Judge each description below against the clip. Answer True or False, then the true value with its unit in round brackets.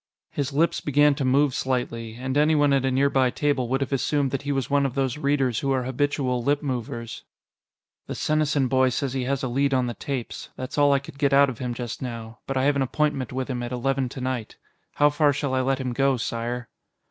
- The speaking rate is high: True (230 wpm)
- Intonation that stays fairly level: True (2.0 semitones)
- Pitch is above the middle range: False (135 Hz)